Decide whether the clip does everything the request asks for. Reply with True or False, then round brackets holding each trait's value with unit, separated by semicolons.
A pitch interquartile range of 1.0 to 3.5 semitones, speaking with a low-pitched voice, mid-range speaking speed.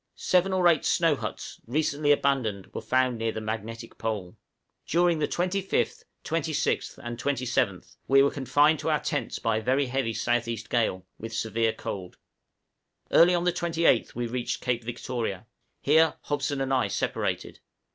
False (5.3 semitones; 130 Hz; 160 wpm)